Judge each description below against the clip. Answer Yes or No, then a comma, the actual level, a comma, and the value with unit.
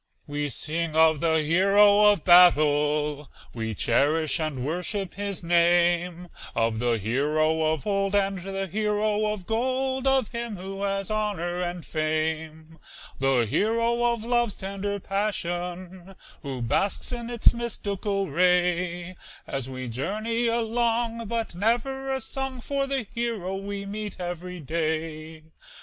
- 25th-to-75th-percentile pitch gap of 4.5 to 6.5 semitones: Yes, average, 5.1 semitones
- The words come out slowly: Yes, slow, 130 wpm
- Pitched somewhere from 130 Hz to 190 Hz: Yes, medium, 185 Hz